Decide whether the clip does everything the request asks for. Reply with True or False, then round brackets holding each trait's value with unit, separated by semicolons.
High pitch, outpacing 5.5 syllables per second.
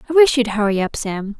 True (235 Hz; 5.9 syllables/s)